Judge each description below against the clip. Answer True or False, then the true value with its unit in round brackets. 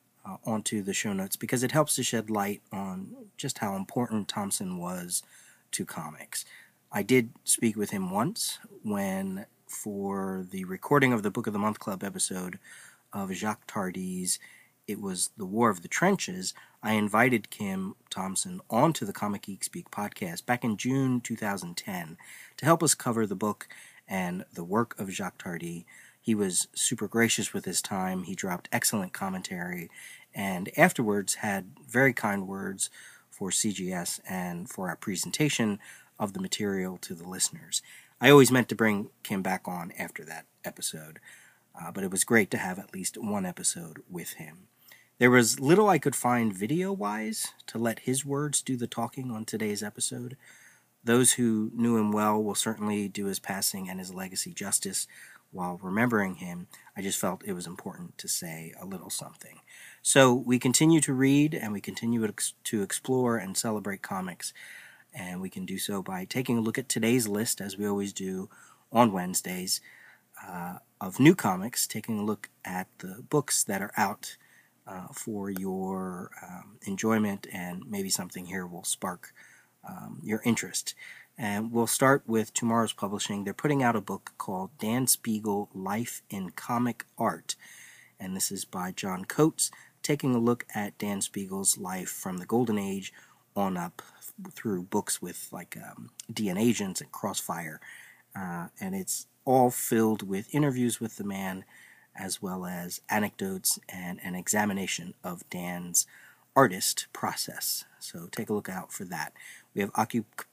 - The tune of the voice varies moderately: True (5.0 semitones)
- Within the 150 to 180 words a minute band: True (165 wpm)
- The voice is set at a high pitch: False (110 Hz)